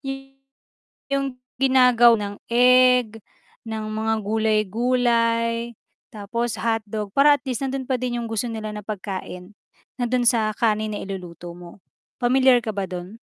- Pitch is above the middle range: Yes, high, 230 Hz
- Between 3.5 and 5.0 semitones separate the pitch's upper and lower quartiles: No, average, 2.9 semitones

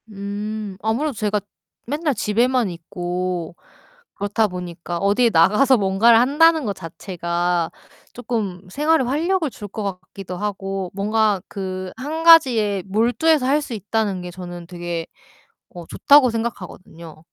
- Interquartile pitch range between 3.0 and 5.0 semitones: No, wide, 5.4 semitones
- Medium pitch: No, high, 205 Hz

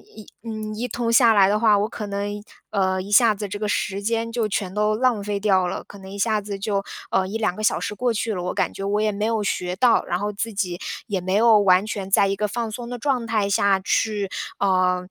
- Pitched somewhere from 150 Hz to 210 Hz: Yes, high, 205 Hz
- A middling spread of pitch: No, narrow, 2.1 semitones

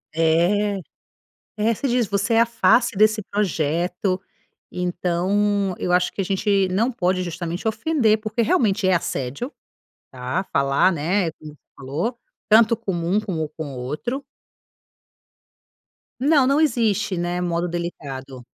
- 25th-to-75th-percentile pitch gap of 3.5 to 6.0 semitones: Yes, average, 4.2 semitones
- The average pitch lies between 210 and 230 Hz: No, high, 190 Hz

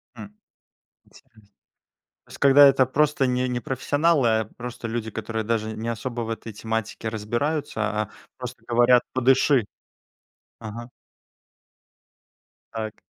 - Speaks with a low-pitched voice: Yes, low, 120 Hz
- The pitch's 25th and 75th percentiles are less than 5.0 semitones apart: Yes, average, 2.8 semitones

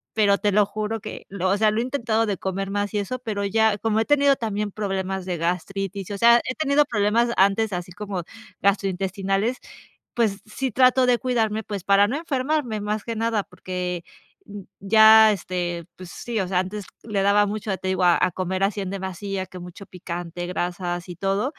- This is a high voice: Yes, high, 200 Hz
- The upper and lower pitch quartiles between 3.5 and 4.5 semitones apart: No, average, 2.9 semitones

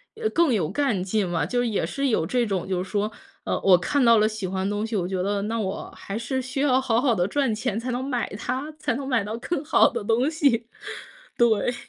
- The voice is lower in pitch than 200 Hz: No, high, 230 Hz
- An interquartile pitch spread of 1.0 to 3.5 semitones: No, average, 4.6 semitones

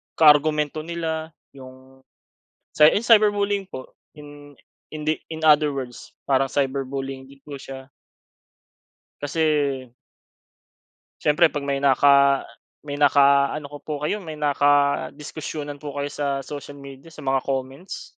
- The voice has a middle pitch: Yes, medium, 145 Hz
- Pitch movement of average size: No, narrow, 2.0 semitones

